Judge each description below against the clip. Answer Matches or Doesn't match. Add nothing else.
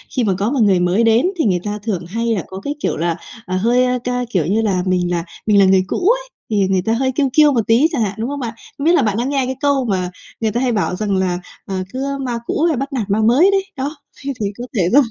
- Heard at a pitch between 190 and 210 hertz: Doesn't match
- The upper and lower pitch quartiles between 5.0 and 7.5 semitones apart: Matches